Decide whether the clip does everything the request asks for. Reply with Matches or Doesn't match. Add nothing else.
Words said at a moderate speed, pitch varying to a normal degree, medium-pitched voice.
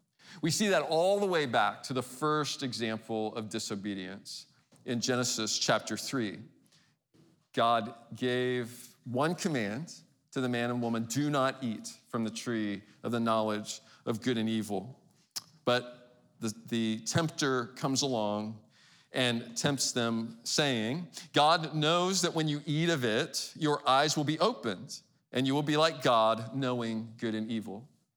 Doesn't match